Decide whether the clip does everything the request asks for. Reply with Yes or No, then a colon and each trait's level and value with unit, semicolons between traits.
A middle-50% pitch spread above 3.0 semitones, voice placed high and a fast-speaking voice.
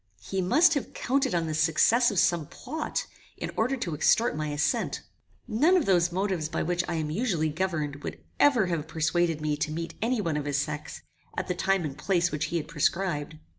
No: average, 4.8 semitones; medium, 170 Hz; fast, 210 wpm